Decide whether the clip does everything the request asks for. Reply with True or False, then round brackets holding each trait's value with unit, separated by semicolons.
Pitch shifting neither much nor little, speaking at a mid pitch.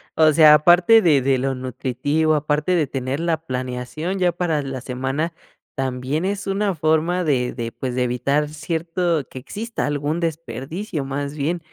True (4.2 semitones; 150 Hz)